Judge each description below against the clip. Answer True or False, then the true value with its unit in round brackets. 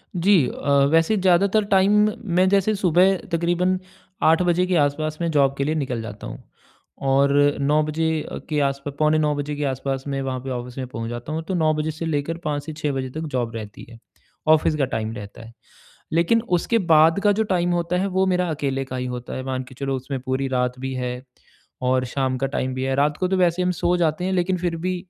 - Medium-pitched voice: True (155 Hz)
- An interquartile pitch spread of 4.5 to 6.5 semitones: True (5.0 semitones)